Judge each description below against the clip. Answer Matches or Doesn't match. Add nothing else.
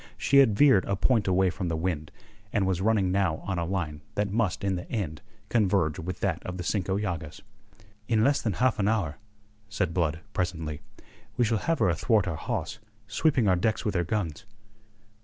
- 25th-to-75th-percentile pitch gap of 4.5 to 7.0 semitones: Doesn't match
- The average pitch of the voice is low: Matches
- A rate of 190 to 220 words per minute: Matches